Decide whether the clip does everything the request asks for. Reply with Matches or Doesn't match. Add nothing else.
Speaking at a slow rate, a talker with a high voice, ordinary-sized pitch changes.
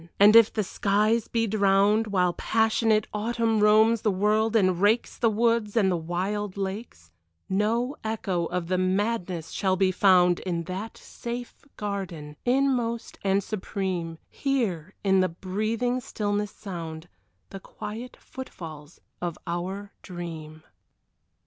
Matches